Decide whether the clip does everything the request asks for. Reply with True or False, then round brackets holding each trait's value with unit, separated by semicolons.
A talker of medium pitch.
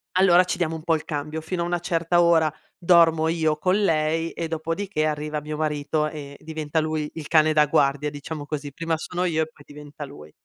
True (155 Hz)